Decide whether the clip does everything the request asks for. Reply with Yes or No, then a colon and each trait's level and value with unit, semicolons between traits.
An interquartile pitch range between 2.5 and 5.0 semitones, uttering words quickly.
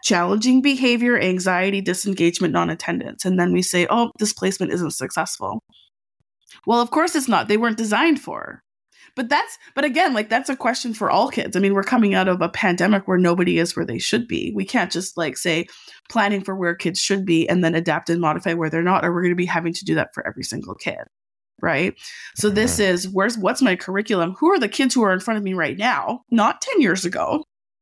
No: wide, 5.5 semitones; fast, 225 wpm